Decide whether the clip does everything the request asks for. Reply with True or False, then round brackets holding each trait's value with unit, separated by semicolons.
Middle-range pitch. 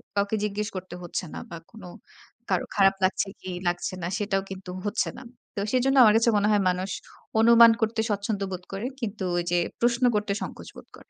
False (205 Hz)